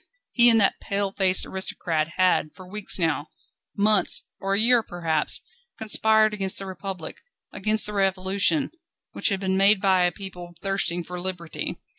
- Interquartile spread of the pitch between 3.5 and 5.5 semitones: No, narrow, 2.4 semitones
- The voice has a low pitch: No, high, 190 Hz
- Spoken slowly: No, average, 155 wpm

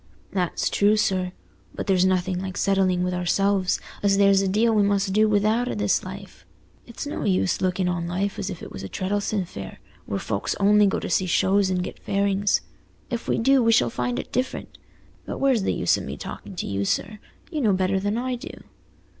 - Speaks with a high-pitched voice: Yes, high, 195 Hz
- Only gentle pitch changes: Yes, narrow, 2.3 semitones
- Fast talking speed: Yes, fast, 210 wpm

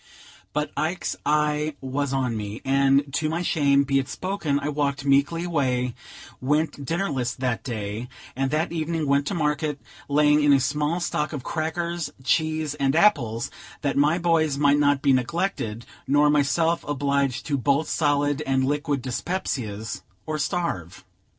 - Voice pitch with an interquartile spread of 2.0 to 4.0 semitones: Yes, narrow, 2.6 semitones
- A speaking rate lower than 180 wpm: Yes, average, 155 wpm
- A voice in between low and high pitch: Yes, medium, 145 Hz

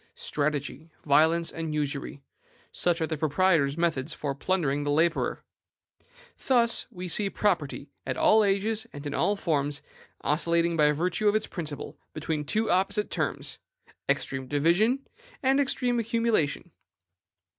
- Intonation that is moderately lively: No, wide, 5.7 semitones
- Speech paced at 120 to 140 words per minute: Yes, slow, 135 wpm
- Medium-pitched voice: Yes, medium, 165 Hz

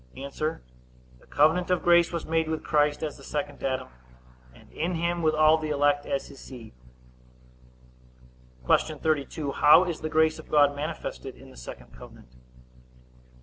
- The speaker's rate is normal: Yes, average, 160 wpm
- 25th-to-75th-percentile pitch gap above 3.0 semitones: No, average, 2.7 semitones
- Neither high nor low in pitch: Yes, medium, 150 Hz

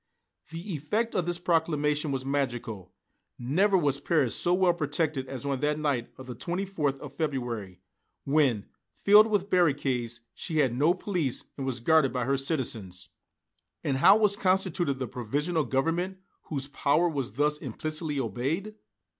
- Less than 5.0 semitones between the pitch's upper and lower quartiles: Yes, average, 4.6 semitones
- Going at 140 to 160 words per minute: Yes, average, 155 wpm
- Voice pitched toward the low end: No, medium, 145 Hz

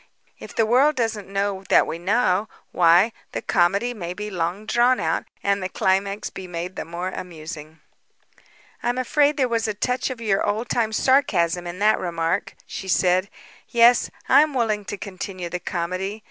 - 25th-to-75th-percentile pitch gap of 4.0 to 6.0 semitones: Yes, average, 4.4 semitones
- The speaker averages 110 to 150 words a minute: No, average, 175 wpm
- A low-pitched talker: No, high, 200 Hz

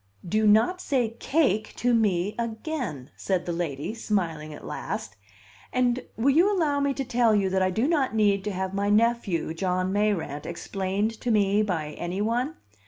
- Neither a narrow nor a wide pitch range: Yes, average, 4.6 semitones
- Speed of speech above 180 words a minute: No, average, 175 wpm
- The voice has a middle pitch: No, high, 210 Hz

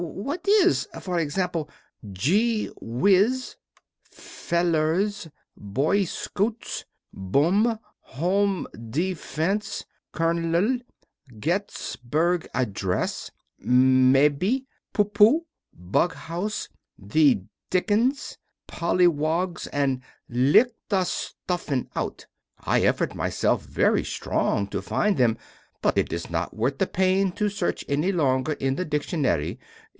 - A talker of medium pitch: Yes, medium, 170 Hz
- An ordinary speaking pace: No, slow, 100 wpm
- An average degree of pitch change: No, wide, 6.9 semitones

